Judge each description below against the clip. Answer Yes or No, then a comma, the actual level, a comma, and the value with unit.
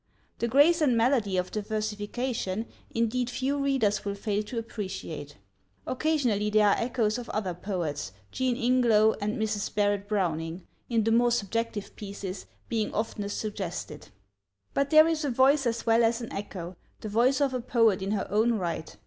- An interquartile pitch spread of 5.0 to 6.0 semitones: No, average, 3.4 semitones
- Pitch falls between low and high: No, high, 220 Hz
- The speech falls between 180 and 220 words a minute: No, average, 170 wpm